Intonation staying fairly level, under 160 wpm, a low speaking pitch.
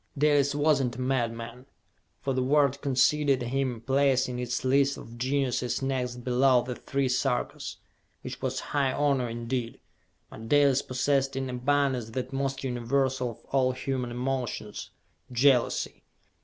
Yes: narrow, 1.9 semitones; average, 140 wpm; low, 130 Hz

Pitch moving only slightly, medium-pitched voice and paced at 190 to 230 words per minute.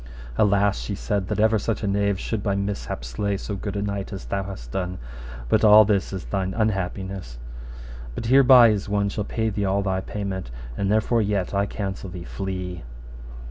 No: narrow, 1.6 semitones; low, 100 Hz; average, 195 wpm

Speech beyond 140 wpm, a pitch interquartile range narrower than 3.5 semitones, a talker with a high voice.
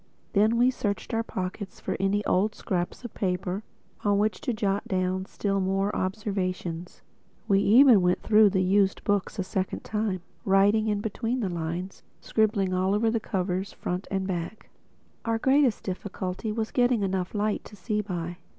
Yes: average, 170 wpm; narrow, 2.5 semitones; high, 200 Hz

